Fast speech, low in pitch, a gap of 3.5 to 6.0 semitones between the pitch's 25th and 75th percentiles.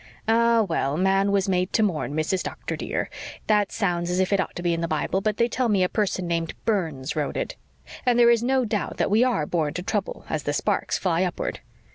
No: fast, 235 wpm; high, 190 Hz; average, 4.3 semitones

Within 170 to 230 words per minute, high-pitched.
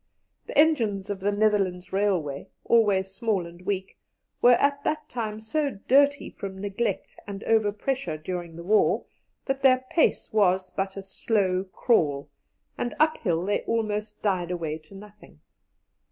No: average, 145 wpm; high, 205 Hz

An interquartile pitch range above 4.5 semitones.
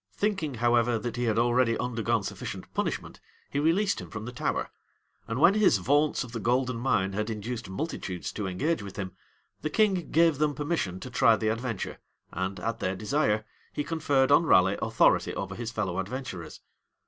Yes: wide, 5.6 semitones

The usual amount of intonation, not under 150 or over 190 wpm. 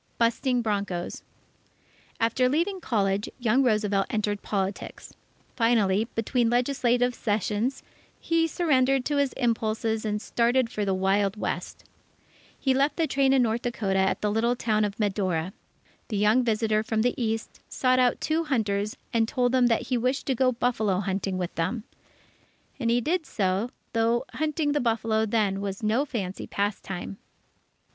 Yes: average, 3.6 semitones; average, 155 wpm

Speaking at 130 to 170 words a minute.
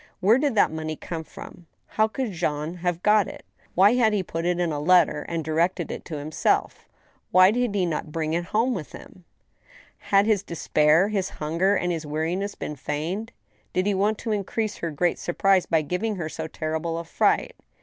No: average, 200 wpm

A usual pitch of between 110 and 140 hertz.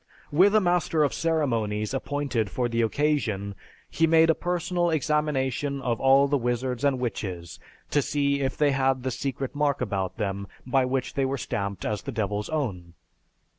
Yes: low, 135 Hz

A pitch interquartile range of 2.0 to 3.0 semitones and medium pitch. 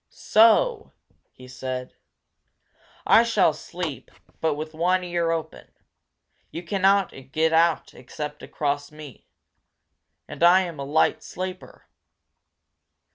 No: average, 3.9 semitones; medium, 165 Hz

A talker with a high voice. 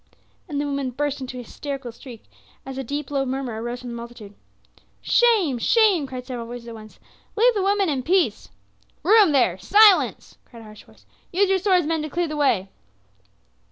Yes: very high, 275 Hz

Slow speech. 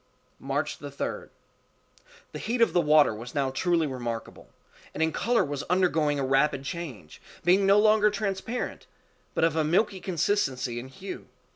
No: average, 155 wpm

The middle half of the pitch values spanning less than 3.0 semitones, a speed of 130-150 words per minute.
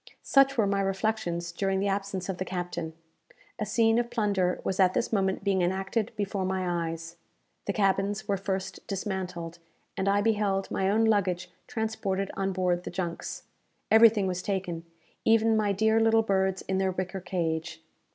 No: narrow, 2.4 semitones; average, 170 wpm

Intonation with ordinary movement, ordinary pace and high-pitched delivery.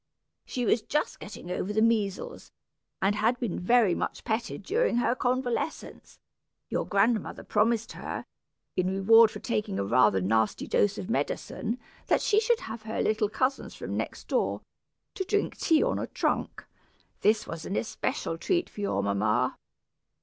Yes: average, 4.4 semitones; average, 160 wpm; high, 220 Hz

